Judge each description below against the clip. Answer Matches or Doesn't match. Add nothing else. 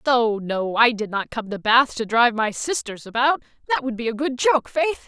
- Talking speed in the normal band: Doesn't match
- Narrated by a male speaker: Doesn't match